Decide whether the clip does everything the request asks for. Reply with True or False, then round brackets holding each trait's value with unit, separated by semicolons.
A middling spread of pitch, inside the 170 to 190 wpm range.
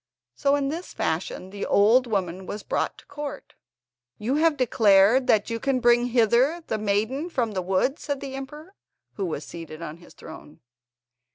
False (5.9 semitones; 175 wpm)